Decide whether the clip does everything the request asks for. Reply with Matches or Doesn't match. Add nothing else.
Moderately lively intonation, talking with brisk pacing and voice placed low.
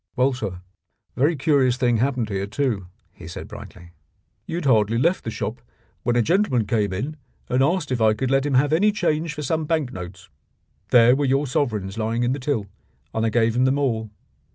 Matches